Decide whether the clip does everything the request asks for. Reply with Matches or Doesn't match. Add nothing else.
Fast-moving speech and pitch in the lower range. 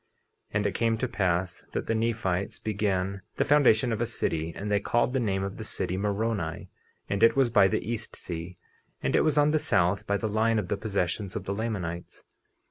Matches